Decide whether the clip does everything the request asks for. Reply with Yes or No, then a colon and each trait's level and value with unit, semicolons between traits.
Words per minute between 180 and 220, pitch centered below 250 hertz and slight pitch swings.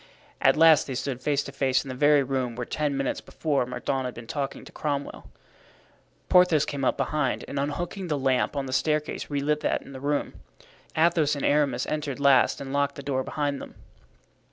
Yes: average, 200 wpm; medium, 140 Hz; narrow, 2.0 semitones